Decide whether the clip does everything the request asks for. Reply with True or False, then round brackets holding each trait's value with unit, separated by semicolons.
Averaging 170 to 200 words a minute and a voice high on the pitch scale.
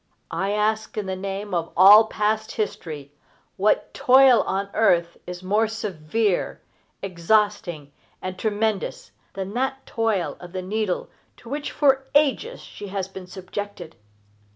False (135 wpm; 205 Hz)